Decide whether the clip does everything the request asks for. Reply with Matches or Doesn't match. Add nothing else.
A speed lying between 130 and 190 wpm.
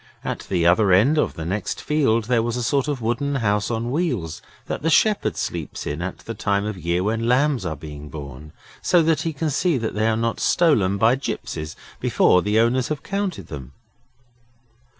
Doesn't match